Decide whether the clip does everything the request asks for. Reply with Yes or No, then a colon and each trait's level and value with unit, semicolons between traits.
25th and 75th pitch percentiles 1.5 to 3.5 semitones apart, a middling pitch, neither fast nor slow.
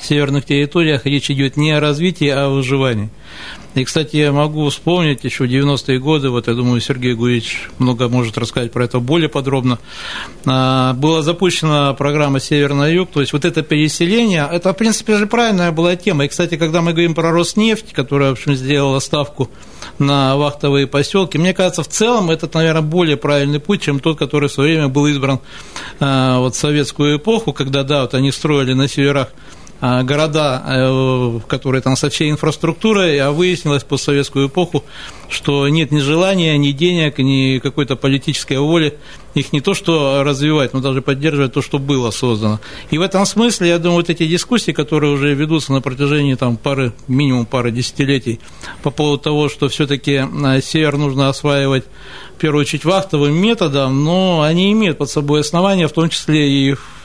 No: average, 2.9 semitones; medium, 145 Hz; fast, 175 wpm